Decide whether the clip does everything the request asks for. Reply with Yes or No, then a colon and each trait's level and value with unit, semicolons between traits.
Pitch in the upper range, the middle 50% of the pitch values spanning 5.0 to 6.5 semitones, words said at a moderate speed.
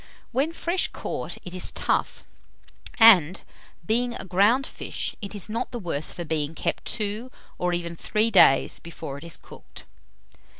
Yes: high, 195 Hz; wide, 5.4 semitones; average, 160 wpm